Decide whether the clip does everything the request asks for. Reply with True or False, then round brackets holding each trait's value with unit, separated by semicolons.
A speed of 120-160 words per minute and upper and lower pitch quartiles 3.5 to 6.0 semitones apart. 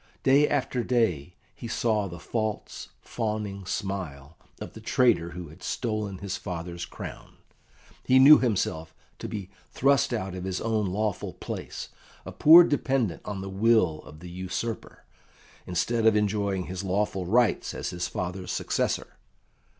True (150 wpm; 4.1 semitones)